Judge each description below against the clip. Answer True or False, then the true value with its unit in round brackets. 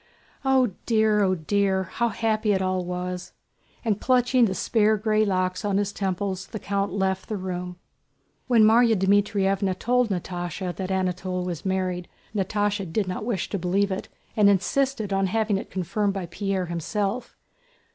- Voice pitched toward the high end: True (195 Hz)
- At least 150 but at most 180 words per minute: True (160 wpm)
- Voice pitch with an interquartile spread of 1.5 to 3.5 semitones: True (2.5 semitones)